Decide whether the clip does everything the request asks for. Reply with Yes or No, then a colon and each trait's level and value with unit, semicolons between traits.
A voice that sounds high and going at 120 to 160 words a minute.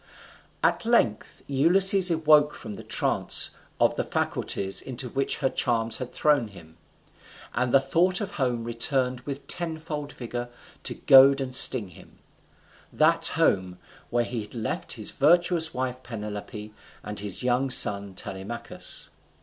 No: low, 125 Hz; average, 140 wpm